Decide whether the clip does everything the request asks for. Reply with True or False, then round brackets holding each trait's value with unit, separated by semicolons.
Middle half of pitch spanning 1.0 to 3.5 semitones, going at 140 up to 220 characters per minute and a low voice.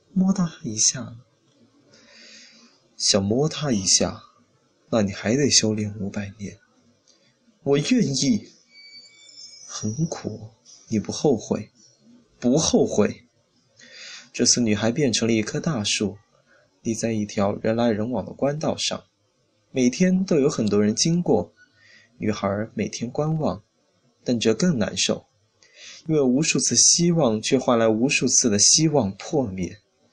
False (5.6 semitones; 180 characters per minute; 115 Hz)